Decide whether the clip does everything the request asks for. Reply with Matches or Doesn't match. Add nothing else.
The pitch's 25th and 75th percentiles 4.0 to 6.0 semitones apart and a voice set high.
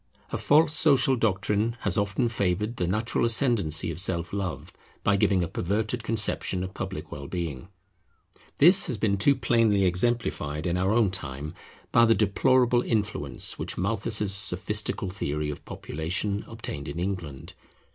Doesn't match